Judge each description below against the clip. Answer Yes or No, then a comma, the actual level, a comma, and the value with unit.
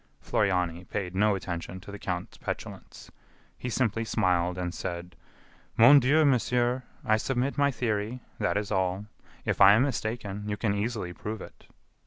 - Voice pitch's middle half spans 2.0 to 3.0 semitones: No, average, 4.6 semitones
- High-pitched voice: No, low, 105 Hz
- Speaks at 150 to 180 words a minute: Yes, average, 160 wpm